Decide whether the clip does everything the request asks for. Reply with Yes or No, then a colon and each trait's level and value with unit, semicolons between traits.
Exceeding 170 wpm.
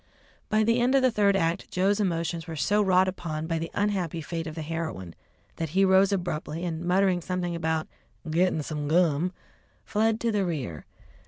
Yes: average, 185 wpm